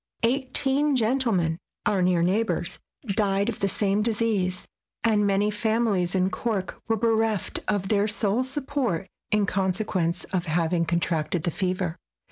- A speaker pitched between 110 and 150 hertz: No, high, 200 Hz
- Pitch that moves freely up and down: No, average, 3.7 semitones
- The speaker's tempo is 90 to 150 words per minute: Yes, average, 140 wpm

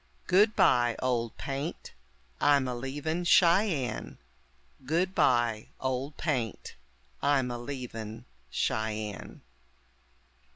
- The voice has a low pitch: Yes, low, 130 Hz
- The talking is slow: Yes, slow, 80 wpm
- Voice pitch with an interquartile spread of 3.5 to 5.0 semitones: Yes, average, 4.4 semitones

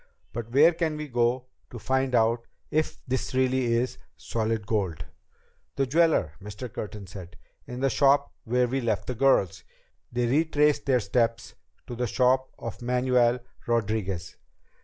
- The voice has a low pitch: Yes, low, 125 Hz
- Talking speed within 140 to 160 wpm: Yes, average, 150 wpm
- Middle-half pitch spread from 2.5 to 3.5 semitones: Yes, average, 2.9 semitones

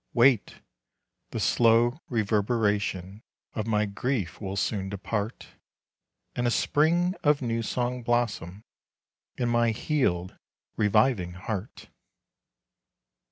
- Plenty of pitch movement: No, average, 3.3 semitones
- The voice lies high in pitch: No, low, 115 Hz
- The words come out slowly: Yes, slow, 100 wpm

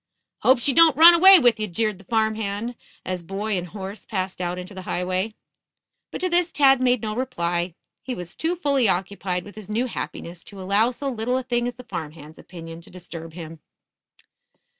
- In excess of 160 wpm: Yes, fast, 205 wpm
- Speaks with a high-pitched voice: Yes, high, 215 Hz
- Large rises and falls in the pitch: Yes, wide, 5.7 semitones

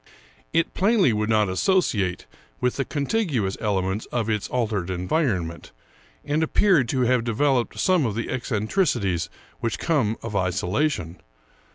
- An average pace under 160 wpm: Yes, average, 140 wpm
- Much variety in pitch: Yes, wide, 6.9 semitones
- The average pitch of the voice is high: No, low, 115 Hz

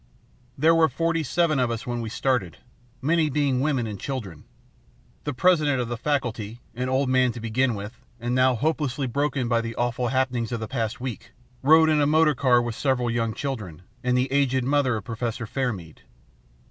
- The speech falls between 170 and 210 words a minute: Yes, average, 190 wpm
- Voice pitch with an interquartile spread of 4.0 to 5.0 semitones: No, average, 3.4 semitones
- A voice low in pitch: Yes, low, 125 Hz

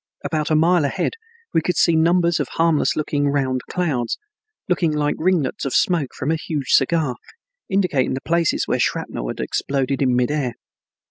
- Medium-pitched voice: Yes, medium, 150 Hz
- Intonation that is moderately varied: Yes, average, 3.7 semitones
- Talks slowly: No, average, 175 wpm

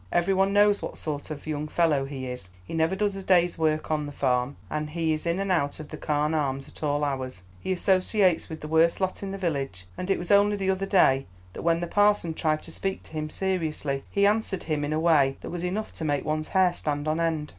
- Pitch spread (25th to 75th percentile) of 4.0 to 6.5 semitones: Yes, average, 4.3 semitones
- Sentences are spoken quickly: Yes, fast, 250 wpm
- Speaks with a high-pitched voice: No, medium, 160 Hz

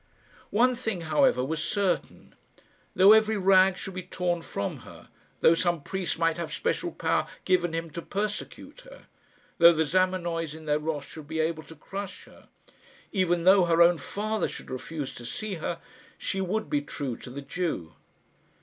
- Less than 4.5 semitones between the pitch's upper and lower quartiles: Yes, average, 3.4 semitones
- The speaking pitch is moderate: Yes, medium, 170 Hz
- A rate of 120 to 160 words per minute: No, average, 175 wpm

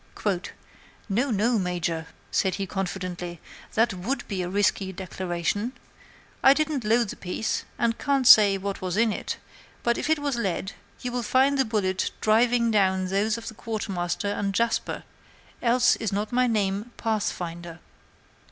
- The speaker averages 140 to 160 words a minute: Yes, average, 155 wpm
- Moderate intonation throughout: Yes, average, 3.9 semitones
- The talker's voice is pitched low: No, high, 210 Hz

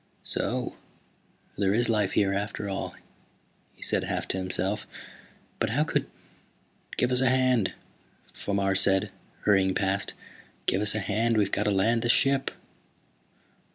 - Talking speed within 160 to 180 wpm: No, average, 150 wpm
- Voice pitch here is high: No, low, 105 Hz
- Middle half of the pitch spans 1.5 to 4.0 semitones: Yes, average, 3.3 semitones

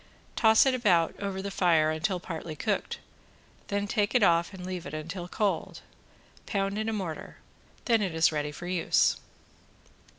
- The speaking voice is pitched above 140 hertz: Yes, medium, 185 Hz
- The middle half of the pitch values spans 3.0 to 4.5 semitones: Yes, average, 3.7 semitones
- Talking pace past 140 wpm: Yes, average, 165 wpm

